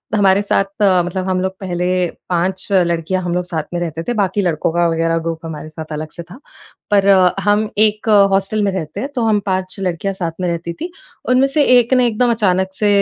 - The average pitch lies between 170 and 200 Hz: Yes, medium, 185 Hz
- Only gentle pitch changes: No, average, 3.3 semitones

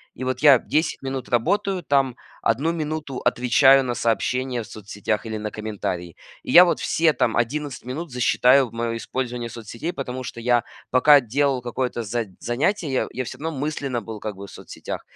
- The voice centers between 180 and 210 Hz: No, low, 125 Hz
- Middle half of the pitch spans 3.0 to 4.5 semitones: Yes, average, 3.6 semitones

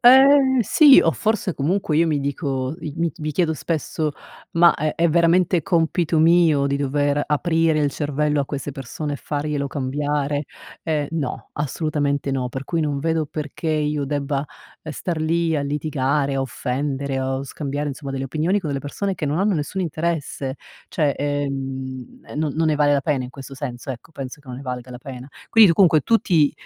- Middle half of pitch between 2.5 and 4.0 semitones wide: Yes, average, 2.9 semitones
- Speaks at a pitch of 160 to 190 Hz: No, medium, 150 Hz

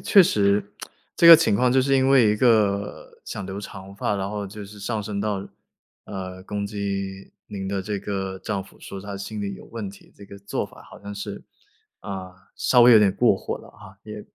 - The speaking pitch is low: Yes, low, 100 Hz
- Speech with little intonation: Yes, narrow, 1.5 semitones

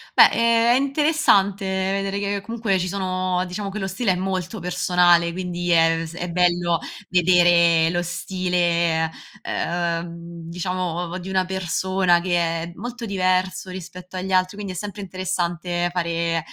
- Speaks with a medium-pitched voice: Yes, medium, 180 Hz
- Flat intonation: Yes, narrow, 1.8 semitones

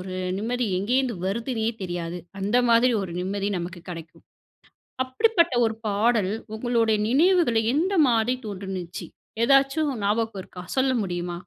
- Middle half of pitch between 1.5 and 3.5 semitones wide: No, average, 5.3 semitones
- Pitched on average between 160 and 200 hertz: No, high, 225 Hz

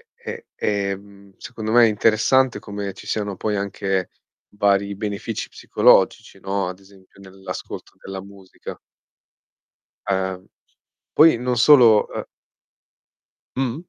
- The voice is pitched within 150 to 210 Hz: No, low, 100 Hz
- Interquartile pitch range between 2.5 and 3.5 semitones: Yes, average, 2.8 semitones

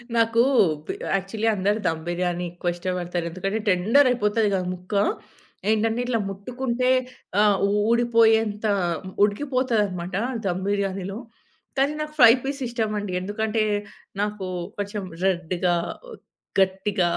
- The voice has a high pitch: Yes, high, 205 Hz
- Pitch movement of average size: Yes, average, 3.6 semitones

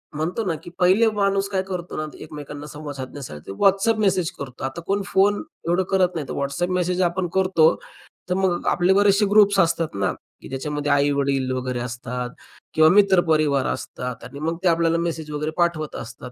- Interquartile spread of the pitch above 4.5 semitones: Yes, average, 5.1 semitones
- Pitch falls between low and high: Yes, medium, 165 Hz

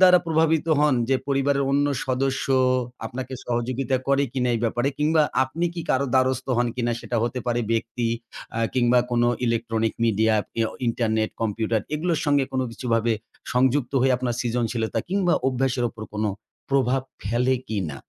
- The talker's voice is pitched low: Yes, low, 125 Hz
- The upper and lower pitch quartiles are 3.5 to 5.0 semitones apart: No, average, 2.8 semitones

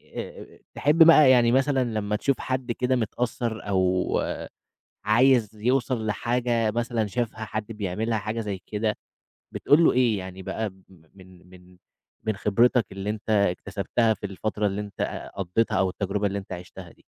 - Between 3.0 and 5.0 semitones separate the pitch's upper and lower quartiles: Yes, average, 3.4 semitones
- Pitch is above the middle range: No, low, 110 Hz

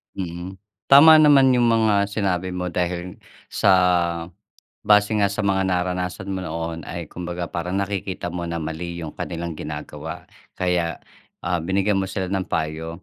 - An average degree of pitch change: No, narrow, 2.3 semitones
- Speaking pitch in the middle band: No, very low, 90 Hz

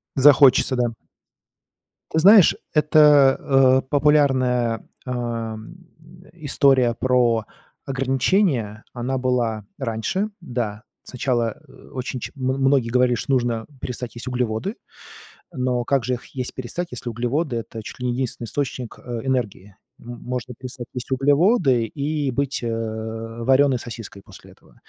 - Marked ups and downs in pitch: No, narrow, 2.5 semitones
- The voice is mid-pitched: No, low, 125 Hz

